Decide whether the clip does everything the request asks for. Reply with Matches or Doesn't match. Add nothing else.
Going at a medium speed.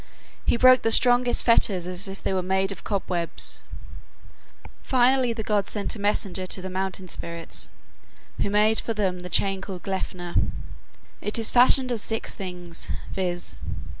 Matches